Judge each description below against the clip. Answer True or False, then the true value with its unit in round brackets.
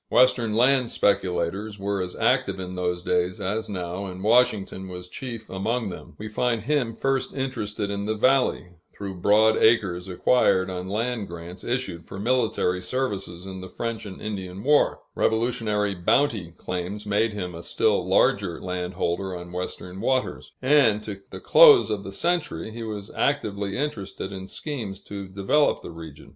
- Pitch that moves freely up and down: False (4.0 semitones)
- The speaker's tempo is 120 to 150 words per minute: False (160 wpm)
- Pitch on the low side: True (100 Hz)